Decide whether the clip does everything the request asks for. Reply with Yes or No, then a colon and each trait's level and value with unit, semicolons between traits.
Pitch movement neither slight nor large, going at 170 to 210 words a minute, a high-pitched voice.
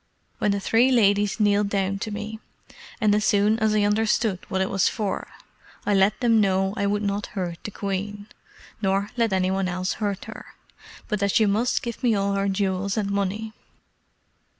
No: narrow, 1.6 semitones; average, 190 wpm; high, 205 Hz